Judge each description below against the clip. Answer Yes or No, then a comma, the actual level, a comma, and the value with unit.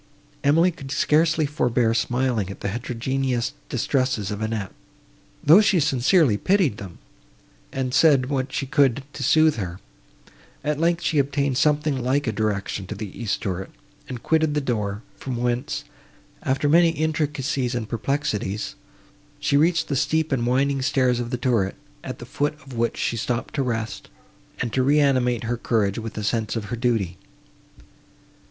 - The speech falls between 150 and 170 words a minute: Yes, average, 160 wpm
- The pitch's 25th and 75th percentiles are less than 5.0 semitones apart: Yes, average, 4.2 semitones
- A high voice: No, low, 130 Hz